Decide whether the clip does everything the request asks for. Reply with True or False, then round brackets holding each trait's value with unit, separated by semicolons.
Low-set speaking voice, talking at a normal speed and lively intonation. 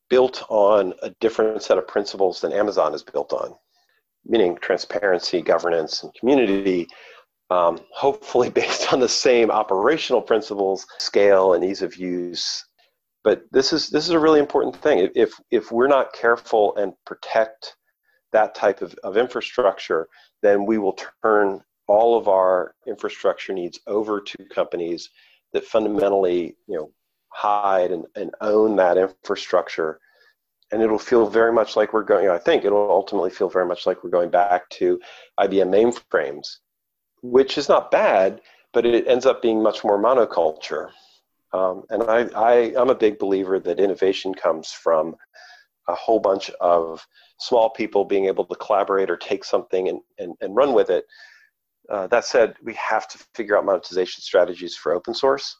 True (110 Hz; 165 wpm; 7.7 semitones)